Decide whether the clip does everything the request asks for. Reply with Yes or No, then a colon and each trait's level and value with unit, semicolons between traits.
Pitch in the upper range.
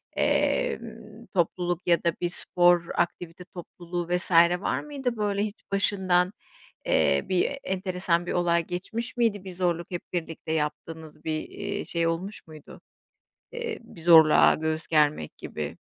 No: medium, 175 Hz